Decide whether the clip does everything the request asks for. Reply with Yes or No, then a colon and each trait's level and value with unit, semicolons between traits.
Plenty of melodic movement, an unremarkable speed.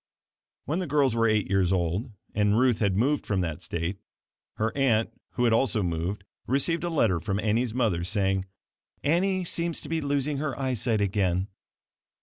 Yes: wide, 6.2 semitones; average, 170 wpm